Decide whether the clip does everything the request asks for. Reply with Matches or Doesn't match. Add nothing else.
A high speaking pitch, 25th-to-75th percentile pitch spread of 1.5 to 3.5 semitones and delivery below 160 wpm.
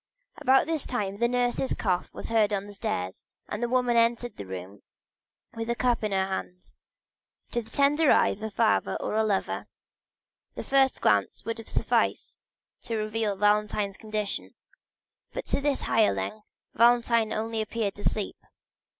Doesn't match